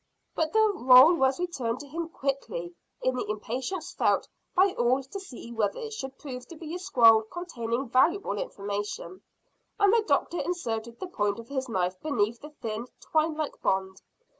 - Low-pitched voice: No, very high, 260 Hz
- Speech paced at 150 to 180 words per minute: Yes, average, 175 wpm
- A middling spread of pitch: No, wide, 6.8 semitones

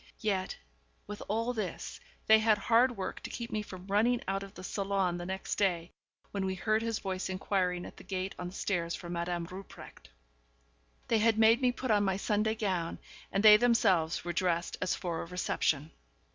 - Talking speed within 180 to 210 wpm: Yes, average, 195 wpm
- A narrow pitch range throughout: No, average, 3.3 semitones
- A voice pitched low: No, high, 195 Hz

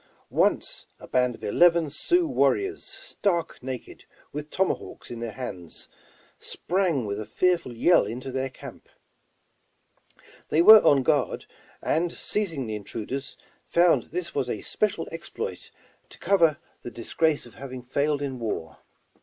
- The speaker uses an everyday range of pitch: No, wide, 5.7 semitones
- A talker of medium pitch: Yes, medium, 145 Hz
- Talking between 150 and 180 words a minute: No, average, 140 wpm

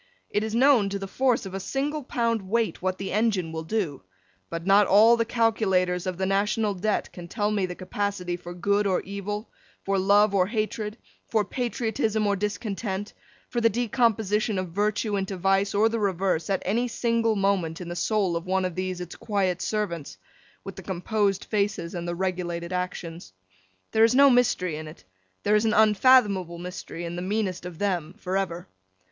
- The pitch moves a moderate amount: Yes, average, 3.2 semitones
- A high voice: Yes, high, 200 Hz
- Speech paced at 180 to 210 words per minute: Yes, average, 190 wpm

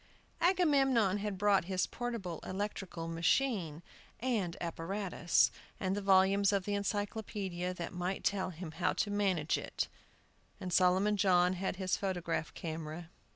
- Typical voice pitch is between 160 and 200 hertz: Yes, high, 190 Hz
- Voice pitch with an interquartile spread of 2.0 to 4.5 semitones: Yes, narrow, 2.6 semitones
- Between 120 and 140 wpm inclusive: Yes, slow, 135 wpm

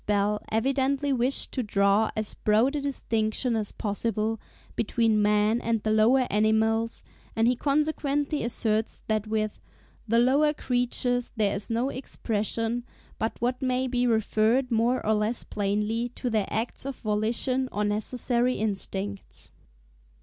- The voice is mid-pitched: No, high, 225 Hz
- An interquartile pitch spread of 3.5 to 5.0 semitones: No, average, 2.8 semitones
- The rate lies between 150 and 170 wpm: No, average, 140 wpm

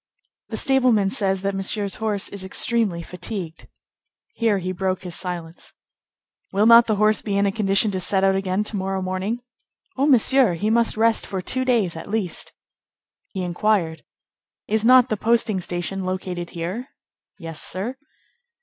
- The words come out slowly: No, average, 160 wpm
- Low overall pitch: No, high, 195 Hz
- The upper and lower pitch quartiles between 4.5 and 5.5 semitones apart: No, average, 3.1 semitones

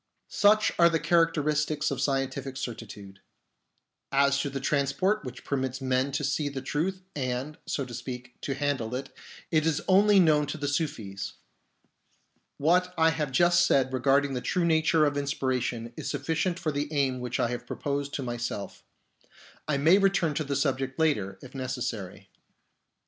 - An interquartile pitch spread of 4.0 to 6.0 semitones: No, average, 3.5 semitones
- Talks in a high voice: No, medium, 140 Hz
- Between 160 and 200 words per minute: Yes, average, 165 wpm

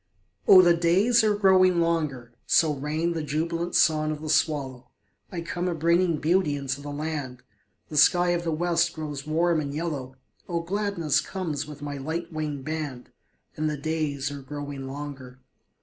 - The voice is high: No, medium, 155 Hz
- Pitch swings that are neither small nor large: Yes, average, 3.0 semitones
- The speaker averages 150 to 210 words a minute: Yes, average, 170 wpm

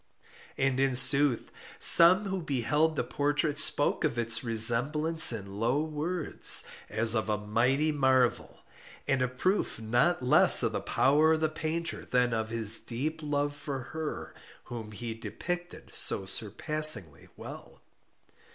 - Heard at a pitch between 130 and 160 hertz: Yes, low, 135 Hz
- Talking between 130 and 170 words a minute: Yes, average, 140 wpm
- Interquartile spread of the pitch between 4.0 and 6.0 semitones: Yes, average, 5.1 semitones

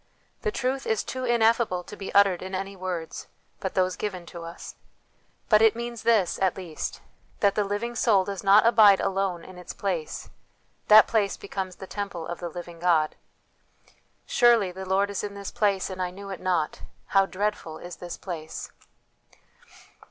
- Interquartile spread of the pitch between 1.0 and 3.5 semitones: Yes, average, 2.7 semitones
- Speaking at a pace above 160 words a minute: Yes, average, 180 wpm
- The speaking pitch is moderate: No, high, 195 Hz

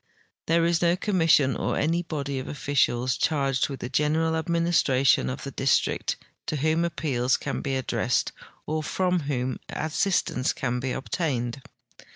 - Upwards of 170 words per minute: No, average, 155 wpm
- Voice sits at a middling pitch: Yes, medium, 145 Hz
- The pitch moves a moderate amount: Yes, average, 4.0 semitones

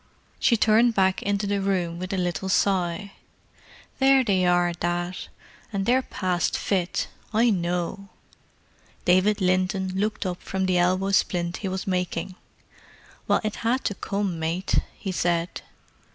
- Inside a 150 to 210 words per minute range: No, average, 140 wpm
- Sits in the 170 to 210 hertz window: Yes, high, 190 Hz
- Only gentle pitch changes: Yes, narrow, 2.3 semitones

